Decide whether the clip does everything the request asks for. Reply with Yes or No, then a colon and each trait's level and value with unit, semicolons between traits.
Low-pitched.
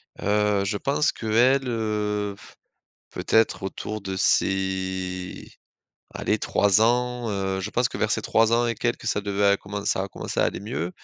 Yes: low, 105 Hz